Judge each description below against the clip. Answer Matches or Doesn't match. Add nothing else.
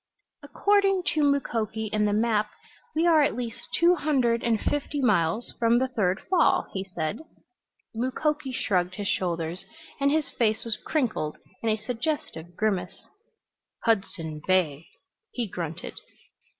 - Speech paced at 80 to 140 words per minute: Matches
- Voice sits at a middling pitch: Doesn't match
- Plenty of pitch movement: Matches